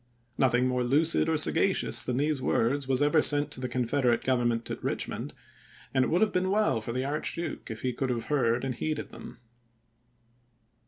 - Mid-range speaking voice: No, low, 130 Hz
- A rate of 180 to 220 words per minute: Yes, average, 190 wpm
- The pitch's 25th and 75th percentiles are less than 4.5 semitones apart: Yes, average, 3.6 semitones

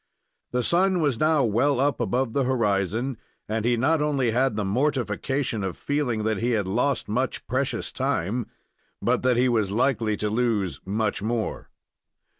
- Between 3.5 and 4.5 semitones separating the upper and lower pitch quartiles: Yes, average, 3.9 semitones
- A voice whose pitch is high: No, low, 120 Hz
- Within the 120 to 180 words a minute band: Yes, average, 165 wpm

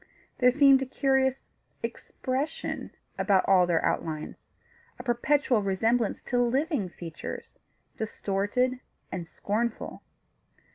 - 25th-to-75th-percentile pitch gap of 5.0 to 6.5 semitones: Yes, average, 5.3 semitones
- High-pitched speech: Yes, high, 240 Hz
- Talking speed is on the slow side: Yes, slow, 100 wpm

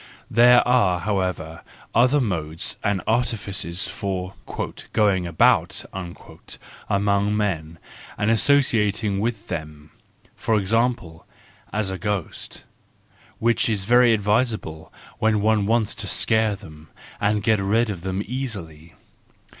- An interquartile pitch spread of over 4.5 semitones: No, average, 3.4 semitones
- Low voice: Yes, low, 105 Hz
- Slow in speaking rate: Yes, slow, 115 wpm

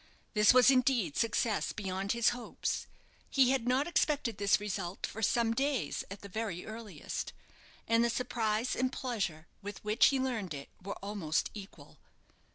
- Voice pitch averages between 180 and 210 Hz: No, high, 220 Hz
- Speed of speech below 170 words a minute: Yes, average, 160 wpm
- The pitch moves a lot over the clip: No, average, 3.9 semitones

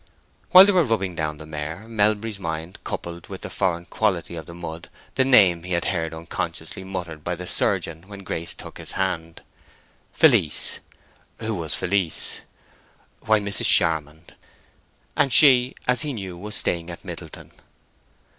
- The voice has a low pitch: Yes, very low, 90 Hz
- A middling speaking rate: Yes, average, 155 wpm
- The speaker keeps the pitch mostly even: No, average, 4.3 semitones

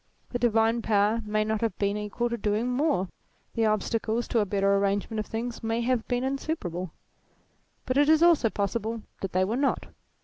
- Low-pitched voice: No, high, 225 Hz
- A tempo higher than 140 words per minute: Yes, average, 195 wpm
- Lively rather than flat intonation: No, average, 2.9 semitones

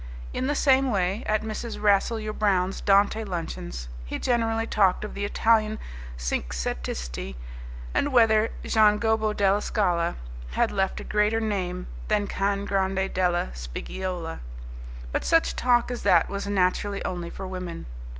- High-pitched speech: Yes, high, 200 Hz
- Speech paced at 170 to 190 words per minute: No, average, 140 wpm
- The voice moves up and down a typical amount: Yes, average, 3.2 semitones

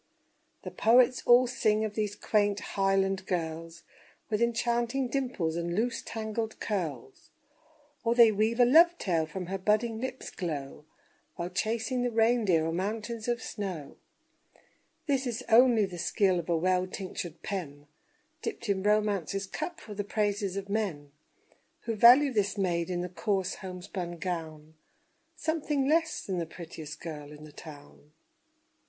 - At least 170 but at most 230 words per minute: No, average, 150 wpm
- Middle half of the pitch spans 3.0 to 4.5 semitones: No, average, 5.2 semitones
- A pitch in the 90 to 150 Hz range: No, high, 200 Hz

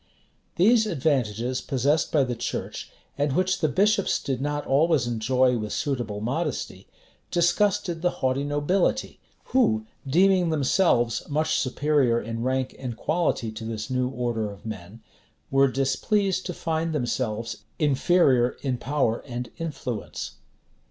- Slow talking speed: Yes, slow, 130 wpm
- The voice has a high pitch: No, low, 135 Hz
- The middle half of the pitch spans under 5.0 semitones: No, wide, 5.4 semitones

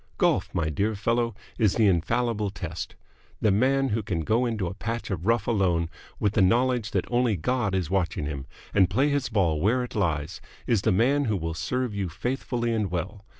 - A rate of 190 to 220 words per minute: Yes, average, 200 wpm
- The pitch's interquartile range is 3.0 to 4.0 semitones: No, average, 4.6 semitones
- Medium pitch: No, low, 105 Hz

